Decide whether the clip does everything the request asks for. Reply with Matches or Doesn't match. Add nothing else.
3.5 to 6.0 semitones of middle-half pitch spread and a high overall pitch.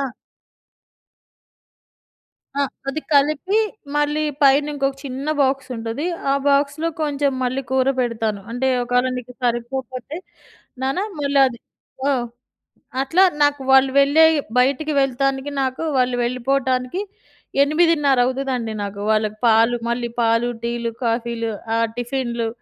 Doesn't match